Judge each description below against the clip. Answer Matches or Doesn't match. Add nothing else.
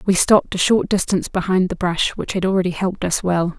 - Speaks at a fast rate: Matches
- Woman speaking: Matches